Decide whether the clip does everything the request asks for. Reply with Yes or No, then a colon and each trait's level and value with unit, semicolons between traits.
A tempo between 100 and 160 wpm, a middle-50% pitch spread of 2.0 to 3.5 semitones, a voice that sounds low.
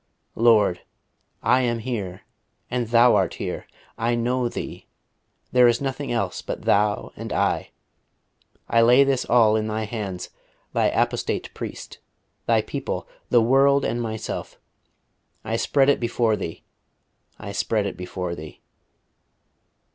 Yes: slow, 135 wpm; average, 3.0 semitones; low, 115 Hz